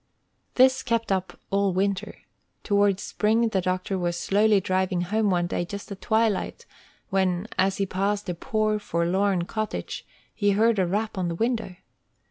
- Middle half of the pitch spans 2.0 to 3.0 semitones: Yes, average, 2.7 semitones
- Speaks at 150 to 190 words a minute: Yes, average, 160 wpm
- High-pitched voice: Yes, high, 200 Hz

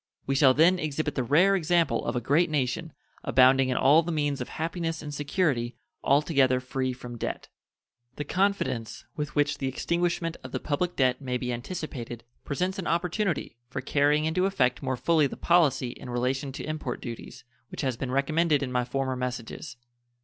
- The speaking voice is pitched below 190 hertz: Yes, medium, 140 Hz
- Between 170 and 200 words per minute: Yes, average, 180 wpm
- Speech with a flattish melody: No, average, 4.2 semitones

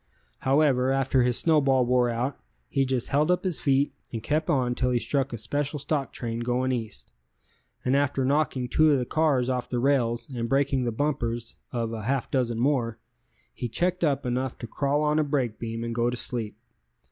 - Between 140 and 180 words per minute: No, average, 200 wpm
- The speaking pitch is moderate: No, low, 130 Hz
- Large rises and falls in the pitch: No, average, 3.1 semitones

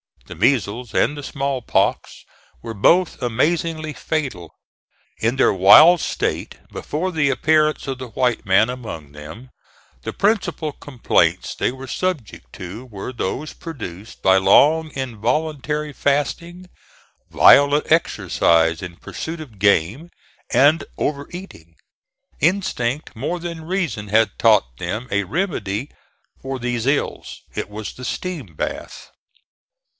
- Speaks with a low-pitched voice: Yes, low, 130 Hz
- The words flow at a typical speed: No, slow, 125 wpm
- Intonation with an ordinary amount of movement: No, wide, 7.0 semitones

